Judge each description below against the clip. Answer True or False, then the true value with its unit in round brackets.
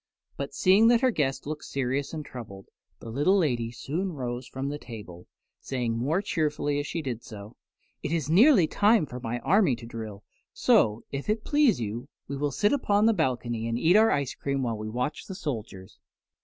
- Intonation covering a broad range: True (6.6 semitones)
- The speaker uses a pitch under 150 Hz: True (140 Hz)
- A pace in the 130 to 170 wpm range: False (195 wpm)